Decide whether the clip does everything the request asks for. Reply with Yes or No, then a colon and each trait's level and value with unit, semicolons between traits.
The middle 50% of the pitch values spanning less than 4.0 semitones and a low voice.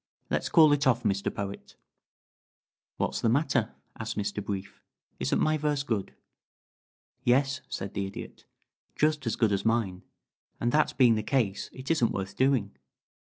No: wide, 5.6 semitones; low, 115 Hz